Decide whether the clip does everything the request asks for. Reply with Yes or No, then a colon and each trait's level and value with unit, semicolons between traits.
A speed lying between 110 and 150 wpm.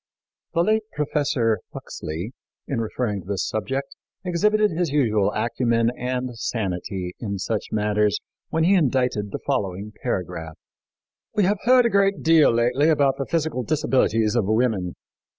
Yes: average, 145 wpm